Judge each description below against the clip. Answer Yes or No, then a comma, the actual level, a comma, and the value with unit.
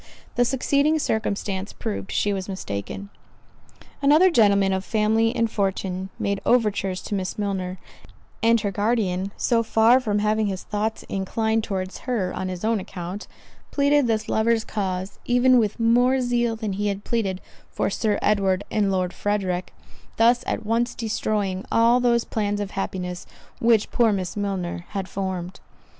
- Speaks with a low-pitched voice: No, high, 210 Hz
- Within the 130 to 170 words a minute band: Yes, average, 155 wpm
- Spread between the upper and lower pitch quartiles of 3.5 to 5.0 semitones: No, average, 3.1 semitones